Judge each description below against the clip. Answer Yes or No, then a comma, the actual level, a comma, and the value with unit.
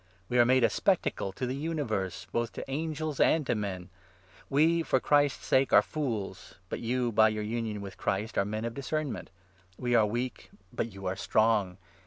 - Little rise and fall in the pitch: No, average, 4.5 semitones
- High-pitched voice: No, low, 120 Hz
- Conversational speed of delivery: Yes, average, 195 wpm